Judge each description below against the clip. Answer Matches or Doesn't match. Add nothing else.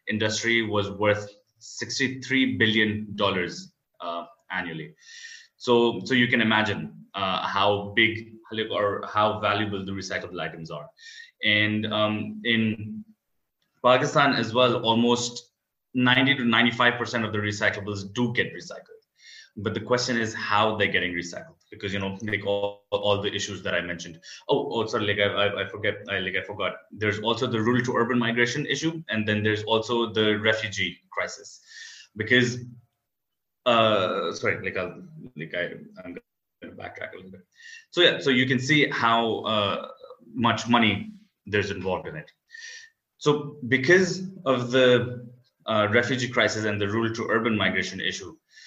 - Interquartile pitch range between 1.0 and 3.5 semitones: Matches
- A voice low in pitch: Matches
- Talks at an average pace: Matches